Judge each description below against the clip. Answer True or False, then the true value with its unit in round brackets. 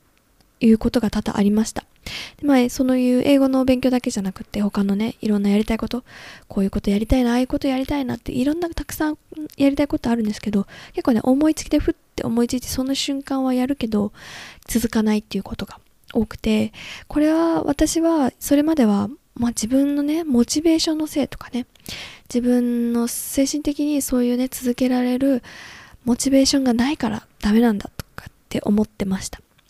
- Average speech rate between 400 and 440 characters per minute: True (405 characters per minute)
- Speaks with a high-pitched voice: True (250 Hz)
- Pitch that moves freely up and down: False (4.0 semitones)